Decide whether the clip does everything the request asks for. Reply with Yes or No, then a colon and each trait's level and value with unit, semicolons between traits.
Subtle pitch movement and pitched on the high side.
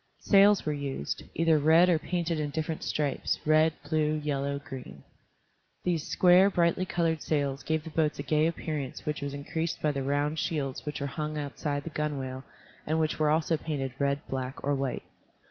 No: narrow, 2.3 semitones; medium, 150 Hz